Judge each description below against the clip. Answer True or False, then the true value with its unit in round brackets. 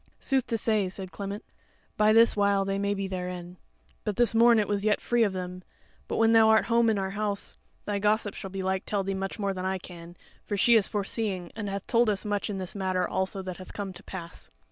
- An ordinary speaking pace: False (235 wpm)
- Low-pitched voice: False (200 Hz)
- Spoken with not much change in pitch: True (2.2 semitones)